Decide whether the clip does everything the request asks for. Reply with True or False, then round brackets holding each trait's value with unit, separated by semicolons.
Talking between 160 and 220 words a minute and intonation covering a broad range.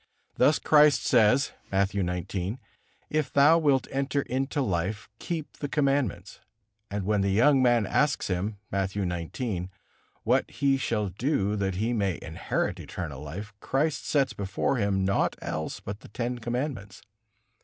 False (145 wpm; 5.9 semitones)